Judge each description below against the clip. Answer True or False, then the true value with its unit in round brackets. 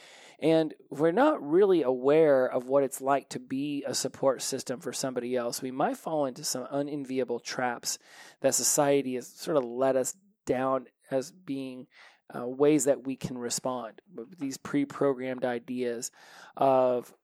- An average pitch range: False (2.3 semitones)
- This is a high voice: False (135 Hz)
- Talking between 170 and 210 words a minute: False (155 wpm)